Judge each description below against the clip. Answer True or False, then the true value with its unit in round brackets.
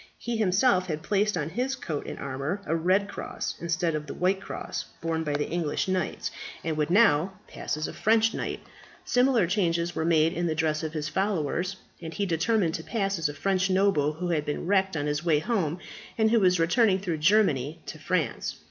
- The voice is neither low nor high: True (170 Hz)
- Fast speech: True (210 wpm)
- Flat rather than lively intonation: False (4.1 semitones)